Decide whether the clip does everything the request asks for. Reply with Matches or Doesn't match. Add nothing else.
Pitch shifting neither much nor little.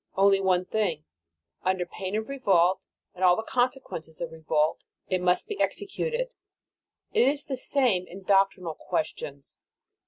Doesn't match